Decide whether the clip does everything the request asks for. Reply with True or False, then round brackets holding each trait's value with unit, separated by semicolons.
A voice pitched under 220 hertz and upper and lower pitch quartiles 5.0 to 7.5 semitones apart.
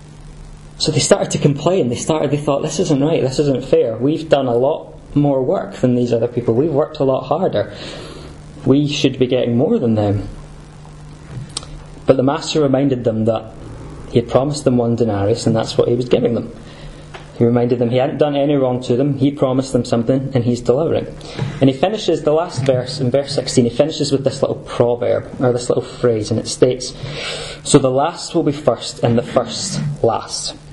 False (135 Hz; 3.2 semitones)